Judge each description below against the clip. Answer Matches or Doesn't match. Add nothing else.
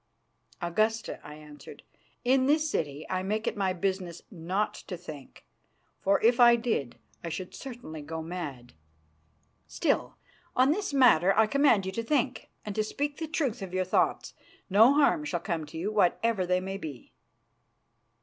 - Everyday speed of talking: Matches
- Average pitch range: Doesn't match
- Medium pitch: Doesn't match